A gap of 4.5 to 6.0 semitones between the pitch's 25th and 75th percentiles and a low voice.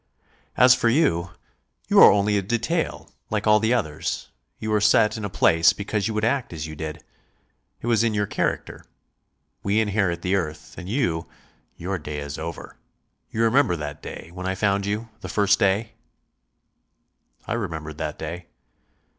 Yes: average, 4.8 semitones; low, 100 Hz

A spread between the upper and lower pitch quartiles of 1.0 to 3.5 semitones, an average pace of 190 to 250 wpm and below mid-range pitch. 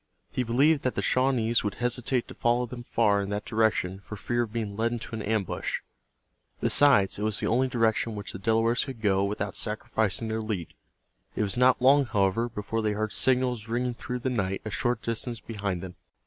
Yes: average, 2.9 semitones; fast, 205 wpm; low, 115 Hz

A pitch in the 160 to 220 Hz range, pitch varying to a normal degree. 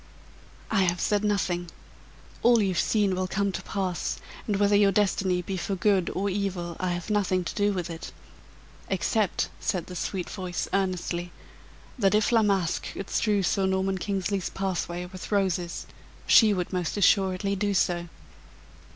No: high, 190 Hz; narrow, 2.1 semitones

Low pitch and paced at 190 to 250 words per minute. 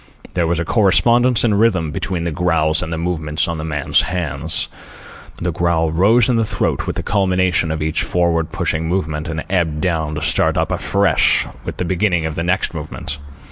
Yes: very low, 85 Hz; average, 195 wpm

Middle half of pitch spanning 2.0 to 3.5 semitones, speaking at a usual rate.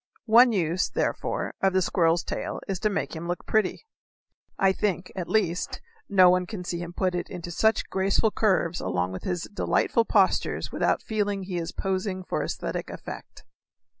Yes: narrow, 2.6 semitones; average, 180 wpm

